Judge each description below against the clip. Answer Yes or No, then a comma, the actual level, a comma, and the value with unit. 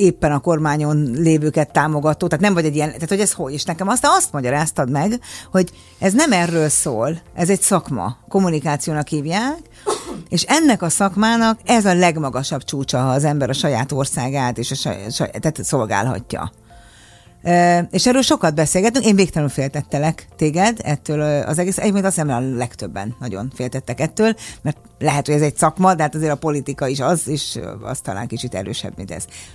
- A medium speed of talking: No, fast, 180 wpm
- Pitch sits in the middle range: Yes, medium, 150 Hz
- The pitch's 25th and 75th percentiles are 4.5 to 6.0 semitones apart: Yes, wide, 5.4 semitones